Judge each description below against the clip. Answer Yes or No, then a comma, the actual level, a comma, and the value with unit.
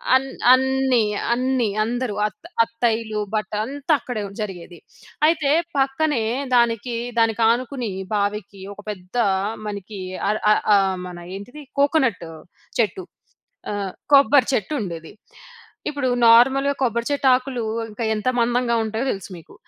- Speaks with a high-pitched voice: Yes, high, 235 Hz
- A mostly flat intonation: No, average, 4.2 semitones